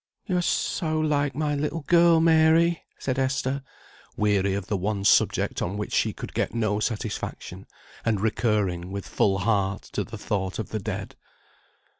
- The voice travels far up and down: Yes, wide, 7.6 semitones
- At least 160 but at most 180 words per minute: Yes, average, 165 wpm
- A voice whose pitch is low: Yes, low, 110 Hz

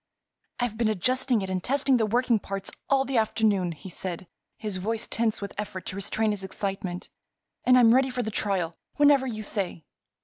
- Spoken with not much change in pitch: No, average, 4.3 semitones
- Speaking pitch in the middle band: No, high, 215 Hz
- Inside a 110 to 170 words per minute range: No, average, 190 wpm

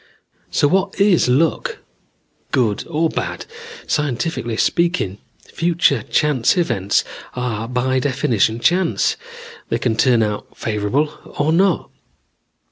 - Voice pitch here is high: No, low, 130 Hz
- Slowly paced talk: Yes, slow, 110 wpm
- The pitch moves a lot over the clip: Yes, wide, 6.5 semitones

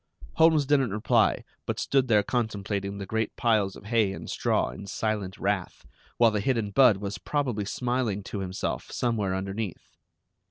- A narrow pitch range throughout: No, average, 3.4 semitones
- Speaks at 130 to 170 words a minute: Yes, average, 160 wpm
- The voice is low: Yes, low, 105 Hz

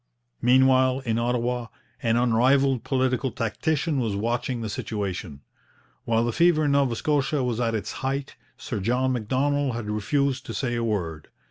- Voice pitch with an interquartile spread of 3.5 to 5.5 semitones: No, average, 3.0 semitones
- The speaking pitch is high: No, low, 125 Hz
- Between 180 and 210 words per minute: No, average, 155 wpm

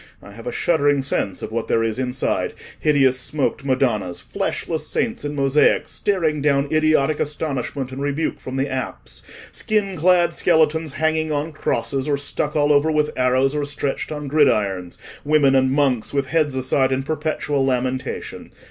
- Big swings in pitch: No, average, 2.8 semitones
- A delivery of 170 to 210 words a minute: No, average, 160 wpm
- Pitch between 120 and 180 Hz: Yes, medium, 140 Hz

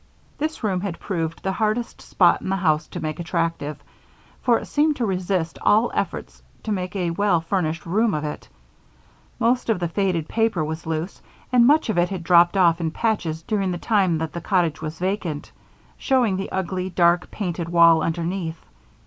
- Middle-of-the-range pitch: Yes, medium, 180 Hz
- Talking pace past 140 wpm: Yes, average, 185 wpm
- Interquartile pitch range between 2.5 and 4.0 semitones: Yes, average, 3.6 semitones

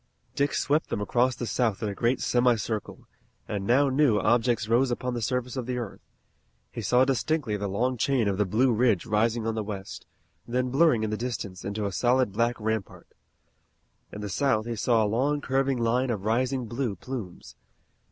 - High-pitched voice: No, low, 120 Hz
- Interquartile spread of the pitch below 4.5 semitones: Yes, average, 3.1 semitones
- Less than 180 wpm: No, average, 195 wpm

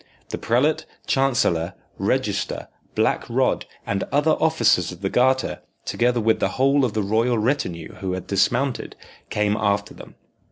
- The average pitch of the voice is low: Yes, low, 115 Hz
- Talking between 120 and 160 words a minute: Yes, average, 150 wpm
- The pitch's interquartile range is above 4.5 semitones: Yes, average, 5.2 semitones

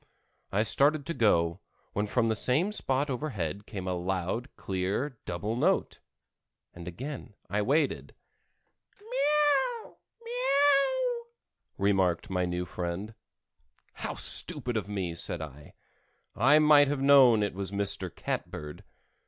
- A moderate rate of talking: No, slow, 125 wpm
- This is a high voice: No, low, 110 Hz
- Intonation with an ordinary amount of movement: No, wide, 8.2 semitones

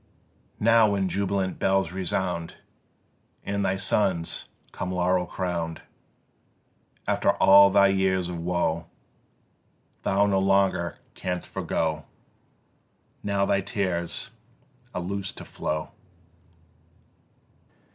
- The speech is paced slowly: Yes, slow, 95 wpm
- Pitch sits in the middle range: No, very low, 95 Hz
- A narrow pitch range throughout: Yes, narrow, 2.1 semitones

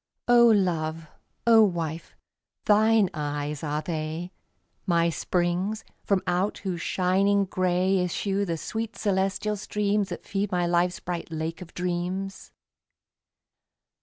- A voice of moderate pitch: Yes, medium, 180 Hz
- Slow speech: Yes, slow, 120 wpm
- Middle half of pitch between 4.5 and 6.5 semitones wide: No, average, 3.0 semitones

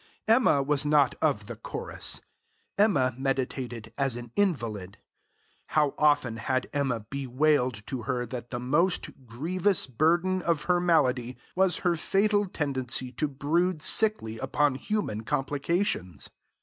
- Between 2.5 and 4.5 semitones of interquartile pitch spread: No, wide, 5.6 semitones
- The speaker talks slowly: Yes, slow, 130 wpm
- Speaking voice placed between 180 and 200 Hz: No, medium, 140 Hz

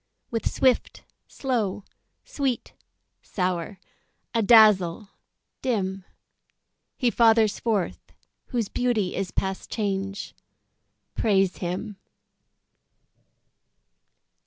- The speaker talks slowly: Yes, slow, 70 wpm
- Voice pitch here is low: No, high, 210 Hz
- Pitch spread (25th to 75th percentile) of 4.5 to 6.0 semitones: No, average, 3.3 semitones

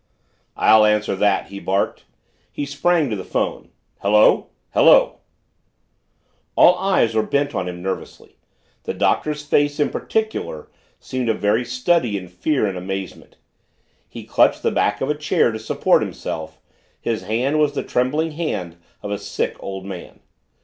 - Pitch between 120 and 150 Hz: No, low, 110 Hz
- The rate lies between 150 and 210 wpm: Yes, average, 155 wpm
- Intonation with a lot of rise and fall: Yes, wide, 6.8 semitones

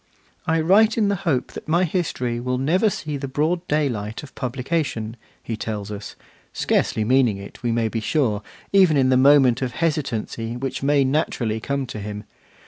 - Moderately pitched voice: No, low, 130 Hz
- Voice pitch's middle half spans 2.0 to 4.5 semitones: No, average, 5.3 semitones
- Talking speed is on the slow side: No, average, 185 wpm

